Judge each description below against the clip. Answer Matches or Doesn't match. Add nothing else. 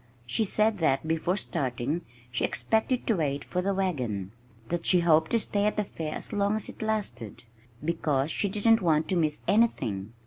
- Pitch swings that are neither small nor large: Doesn't match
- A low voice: Doesn't match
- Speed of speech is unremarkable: Matches